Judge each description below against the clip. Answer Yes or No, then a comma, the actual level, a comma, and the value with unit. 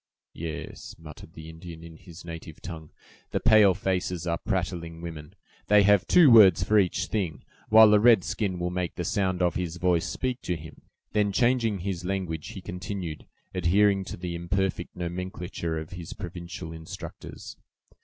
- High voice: No, very low, 90 Hz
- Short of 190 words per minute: Yes, average, 165 wpm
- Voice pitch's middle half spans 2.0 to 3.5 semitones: Yes, average, 2.9 semitones